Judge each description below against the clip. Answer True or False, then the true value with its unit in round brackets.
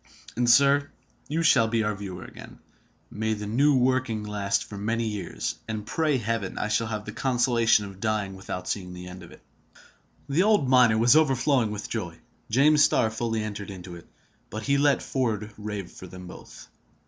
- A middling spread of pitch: True (3.9 semitones)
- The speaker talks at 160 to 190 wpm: True (185 wpm)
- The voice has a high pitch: False (110 Hz)